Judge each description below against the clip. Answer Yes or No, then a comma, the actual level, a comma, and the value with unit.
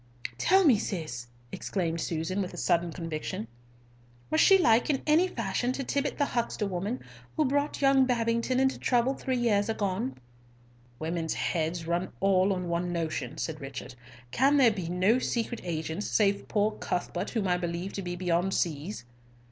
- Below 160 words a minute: No, average, 165 wpm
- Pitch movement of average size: No, wide, 6.2 semitones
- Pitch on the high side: Yes, high, 195 Hz